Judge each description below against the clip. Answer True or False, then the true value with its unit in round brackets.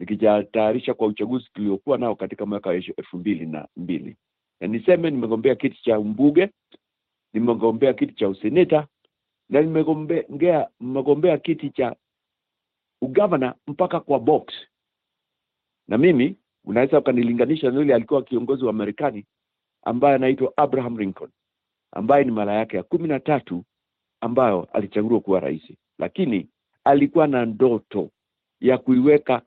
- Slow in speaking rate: False (125 wpm)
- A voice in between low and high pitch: False (130 Hz)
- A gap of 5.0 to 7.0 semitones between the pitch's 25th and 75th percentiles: True (5.3 semitones)